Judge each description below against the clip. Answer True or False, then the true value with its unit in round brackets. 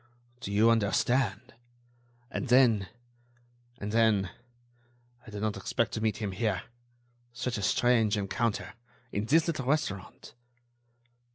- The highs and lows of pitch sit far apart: False (3.2 semitones)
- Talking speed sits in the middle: False (120 wpm)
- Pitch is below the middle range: True (110 Hz)